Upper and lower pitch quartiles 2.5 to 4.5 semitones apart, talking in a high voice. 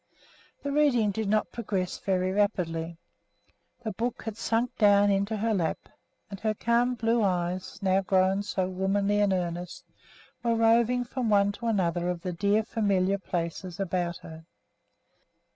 Yes: average, 3.4 semitones; high, 200 Hz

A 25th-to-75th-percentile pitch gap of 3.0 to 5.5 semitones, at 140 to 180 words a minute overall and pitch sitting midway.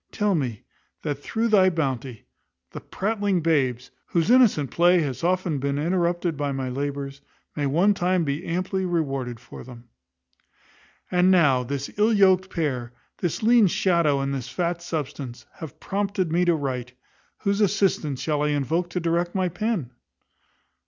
Yes: average, 5.1 semitones; average, 155 wpm; medium, 165 Hz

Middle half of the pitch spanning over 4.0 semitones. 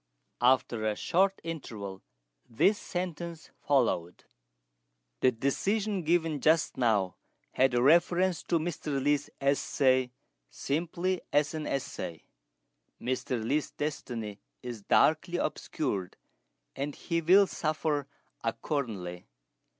Yes: wide, 5.5 semitones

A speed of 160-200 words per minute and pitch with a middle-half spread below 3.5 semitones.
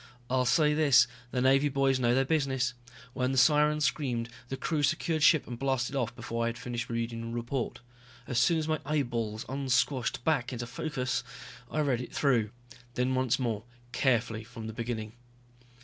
Yes: average, 180 wpm; average, 2.8 semitones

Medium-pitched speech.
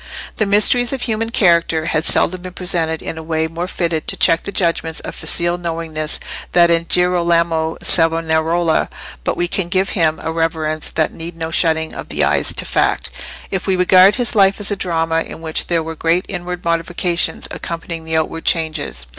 Yes: medium, 165 Hz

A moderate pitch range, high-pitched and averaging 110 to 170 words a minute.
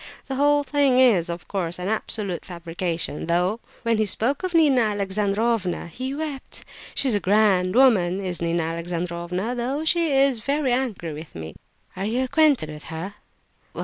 No: wide, 7.0 semitones; high, 210 Hz; average, 160 wpm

